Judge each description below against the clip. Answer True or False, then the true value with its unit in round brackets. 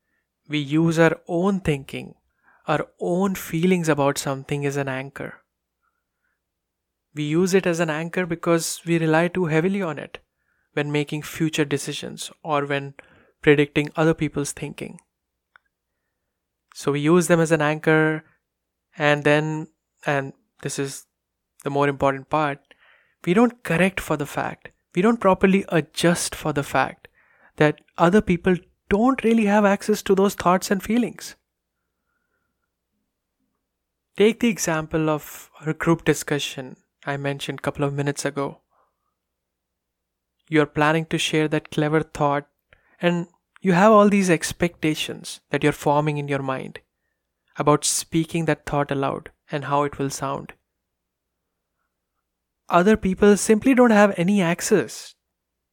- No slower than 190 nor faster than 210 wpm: False (135 wpm)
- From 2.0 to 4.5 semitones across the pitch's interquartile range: True (3.6 semitones)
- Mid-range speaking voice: True (155 Hz)